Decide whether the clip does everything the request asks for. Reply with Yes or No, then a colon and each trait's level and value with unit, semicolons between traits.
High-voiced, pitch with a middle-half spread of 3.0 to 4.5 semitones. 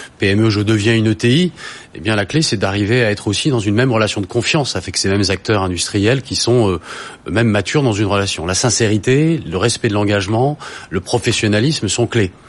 No: low, 110 Hz; average, 3.3 semitones